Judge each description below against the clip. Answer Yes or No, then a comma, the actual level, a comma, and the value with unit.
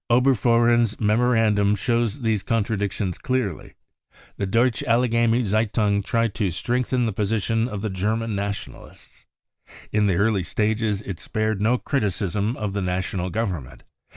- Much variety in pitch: No, narrow, 2.6 semitones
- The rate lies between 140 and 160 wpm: Yes, average, 155 wpm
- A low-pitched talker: Yes, low, 110 Hz